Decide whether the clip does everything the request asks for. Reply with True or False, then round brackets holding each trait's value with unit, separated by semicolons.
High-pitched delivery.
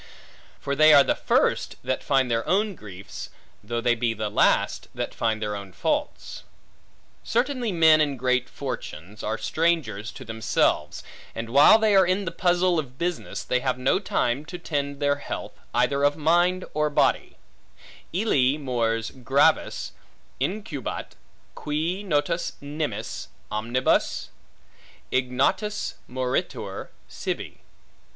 False (140 Hz)